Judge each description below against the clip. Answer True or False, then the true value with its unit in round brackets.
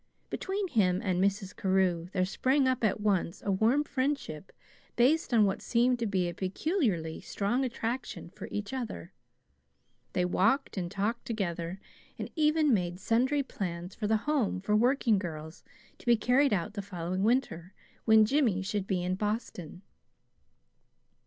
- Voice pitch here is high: True (205 Hz)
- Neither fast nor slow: True (155 wpm)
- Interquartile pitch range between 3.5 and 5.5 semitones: True (5.1 semitones)